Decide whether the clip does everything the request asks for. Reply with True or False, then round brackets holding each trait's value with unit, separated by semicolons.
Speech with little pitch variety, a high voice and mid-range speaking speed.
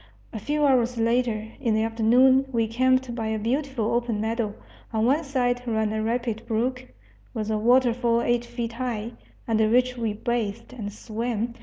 True (2.2 semitones; 235 Hz; 170 wpm)